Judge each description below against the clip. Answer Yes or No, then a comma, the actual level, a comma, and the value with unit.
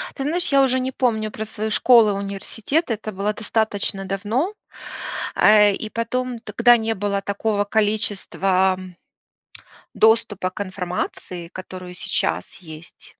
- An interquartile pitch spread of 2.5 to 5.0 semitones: Yes, average, 2.9 semitones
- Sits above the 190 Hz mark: Yes, high, 210 Hz